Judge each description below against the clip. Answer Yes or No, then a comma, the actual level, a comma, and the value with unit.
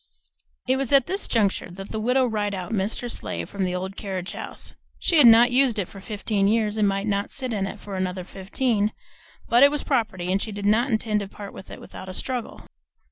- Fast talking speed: Yes, fast, 230 wpm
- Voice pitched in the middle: No, high, 210 Hz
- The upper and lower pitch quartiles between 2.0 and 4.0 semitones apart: Yes, average, 3.5 semitones